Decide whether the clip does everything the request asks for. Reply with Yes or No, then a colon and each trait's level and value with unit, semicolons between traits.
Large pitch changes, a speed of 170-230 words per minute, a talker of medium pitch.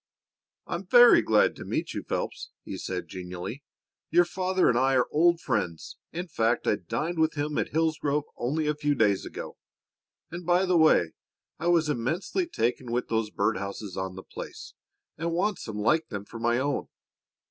Yes: wide, 7.1 semitones; average, 180 wpm; medium, 145 Hz